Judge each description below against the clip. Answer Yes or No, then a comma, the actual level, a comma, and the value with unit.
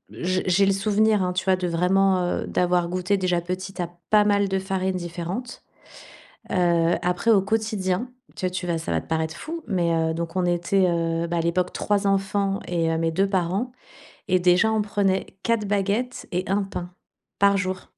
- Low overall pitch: No, medium, 185 Hz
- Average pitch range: No, narrow, 2.3 semitones